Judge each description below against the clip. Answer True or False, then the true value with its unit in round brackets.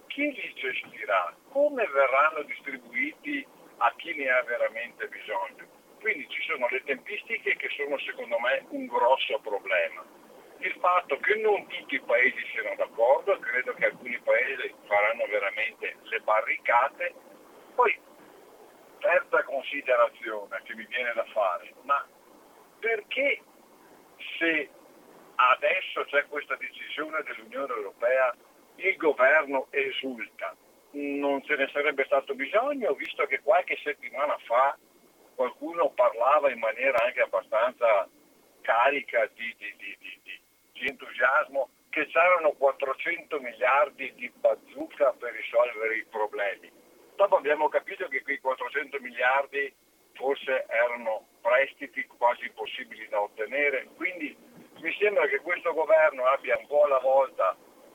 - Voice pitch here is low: False (290 Hz)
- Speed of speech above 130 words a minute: False (125 wpm)